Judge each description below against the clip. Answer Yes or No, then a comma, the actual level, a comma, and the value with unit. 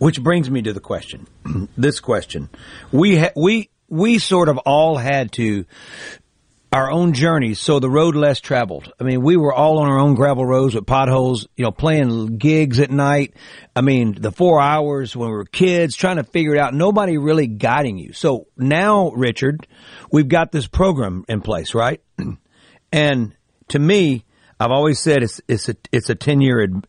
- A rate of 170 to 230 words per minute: Yes, average, 190 wpm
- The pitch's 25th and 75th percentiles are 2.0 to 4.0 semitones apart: No, average, 4.4 semitones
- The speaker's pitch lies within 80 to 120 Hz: No, medium, 140 Hz